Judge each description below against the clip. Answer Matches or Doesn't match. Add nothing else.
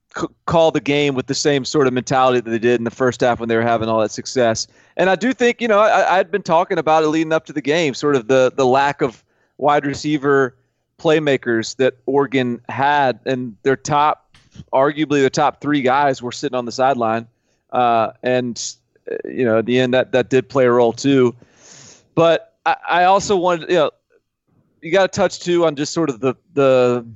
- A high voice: Doesn't match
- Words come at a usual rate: Doesn't match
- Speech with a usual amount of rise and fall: Matches